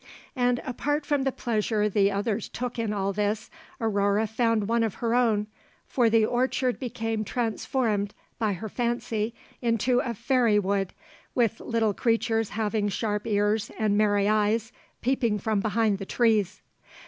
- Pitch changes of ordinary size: No, narrow, 2.3 semitones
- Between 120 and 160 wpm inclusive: Yes, average, 150 wpm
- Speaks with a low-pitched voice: No, high, 220 Hz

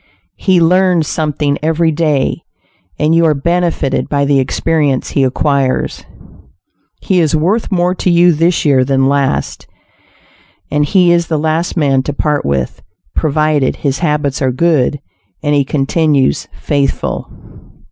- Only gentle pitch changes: No, average, 3.3 semitones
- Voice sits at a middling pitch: Yes, medium, 150 Hz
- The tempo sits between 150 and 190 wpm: No, average, 140 wpm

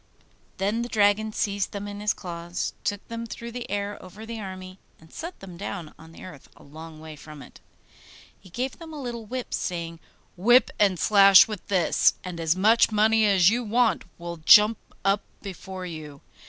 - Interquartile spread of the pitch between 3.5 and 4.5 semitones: Yes, average, 4.2 semitones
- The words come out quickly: No, average, 190 wpm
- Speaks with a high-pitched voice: Yes, high, 200 Hz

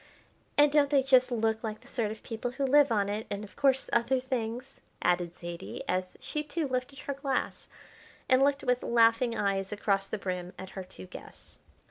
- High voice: Yes, high, 235 Hz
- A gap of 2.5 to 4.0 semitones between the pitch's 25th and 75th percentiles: No, average, 5.1 semitones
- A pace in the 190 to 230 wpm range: Yes, average, 195 wpm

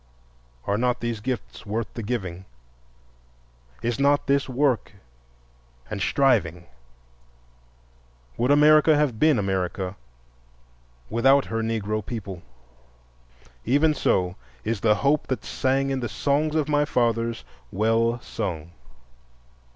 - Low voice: Yes, low, 115 Hz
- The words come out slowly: Yes, slow, 110 wpm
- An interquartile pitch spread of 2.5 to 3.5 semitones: No, average, 4.8 semitones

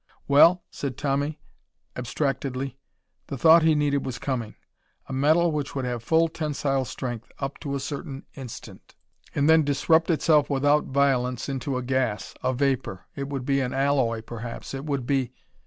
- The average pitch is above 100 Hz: Yes, low, 135 Hz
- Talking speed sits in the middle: Yes, average, 165 wpm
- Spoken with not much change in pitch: Yes, narrow, 2.3 semitones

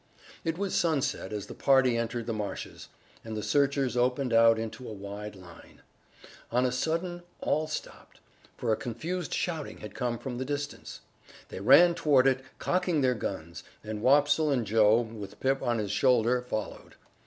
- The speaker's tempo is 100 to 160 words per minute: No, average, 170 wpm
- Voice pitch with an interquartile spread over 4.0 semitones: Yes, average, 4.7 semitones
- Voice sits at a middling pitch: No, low, 125 Hz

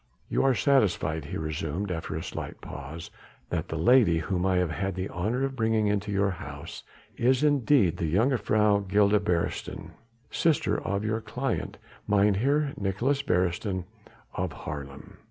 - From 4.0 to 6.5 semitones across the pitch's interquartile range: Yes, average, 4.8 semitones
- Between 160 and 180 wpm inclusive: No, average, 150 wpm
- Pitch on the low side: Yes, low, 100 Hz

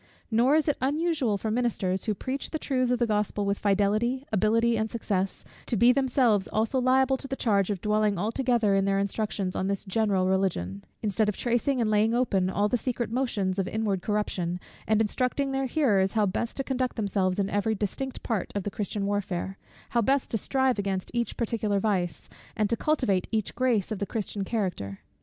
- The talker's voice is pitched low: No, high, 215 Hz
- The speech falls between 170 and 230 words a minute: Yes, average, 195 wpm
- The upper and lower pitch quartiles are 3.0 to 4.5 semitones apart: Yes, average, 3.9 semitones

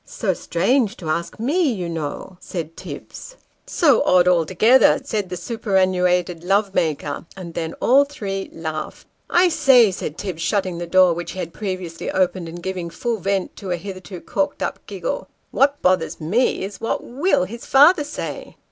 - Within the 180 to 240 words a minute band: Yes, average, 185 wpm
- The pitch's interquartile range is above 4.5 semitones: Yes, average, 5.3 semitones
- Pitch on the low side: No, medium, 185 Hz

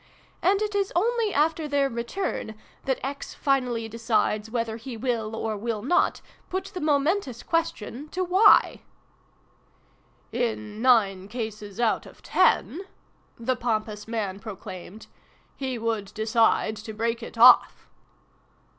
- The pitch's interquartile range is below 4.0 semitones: No, average, 4.6 semitones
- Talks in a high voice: Yes, high, 235 Hz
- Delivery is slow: Yes, slow, 130 wpm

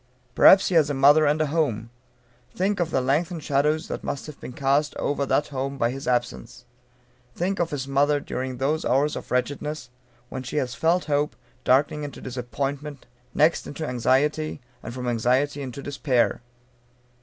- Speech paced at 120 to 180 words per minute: Yes, average, 170 wpm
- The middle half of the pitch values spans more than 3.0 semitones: No, average, 2.7 semitones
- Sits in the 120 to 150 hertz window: Yes, medium, 140 Hz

